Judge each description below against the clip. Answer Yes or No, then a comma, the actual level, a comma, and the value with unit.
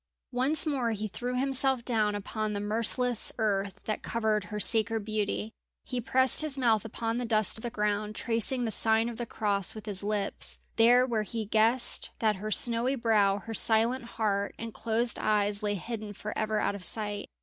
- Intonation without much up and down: Yes, narrow, 2.2 semitones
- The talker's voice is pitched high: Yes, high, 220 Hz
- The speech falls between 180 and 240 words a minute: Yes, average, 190 wpm